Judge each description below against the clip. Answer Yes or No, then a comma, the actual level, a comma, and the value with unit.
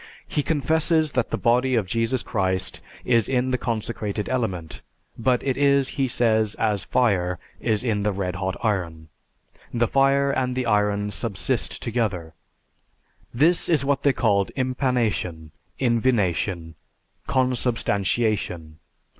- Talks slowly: Yes, slow, 130 wpm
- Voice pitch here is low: Yes, low, 115 Hz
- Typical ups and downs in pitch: Yes, average, 4.6 semitones